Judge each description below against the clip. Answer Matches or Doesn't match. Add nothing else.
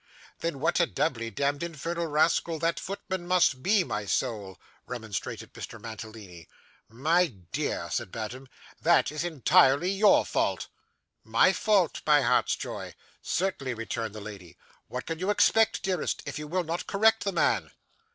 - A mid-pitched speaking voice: Matches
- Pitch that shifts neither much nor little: Doesn't match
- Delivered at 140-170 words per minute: Matches